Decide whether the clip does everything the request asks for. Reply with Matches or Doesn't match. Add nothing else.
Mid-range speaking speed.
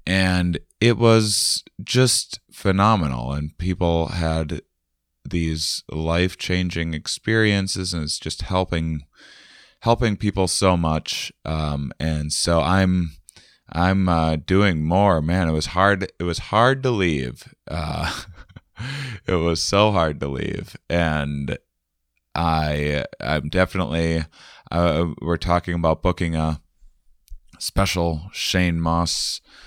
Doesn't match